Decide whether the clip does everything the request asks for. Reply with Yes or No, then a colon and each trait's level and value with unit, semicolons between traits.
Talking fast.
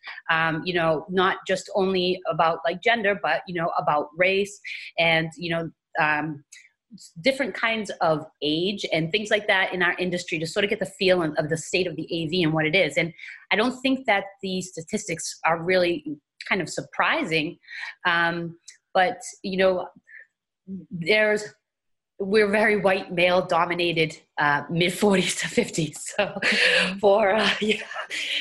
No: average, 160 wpm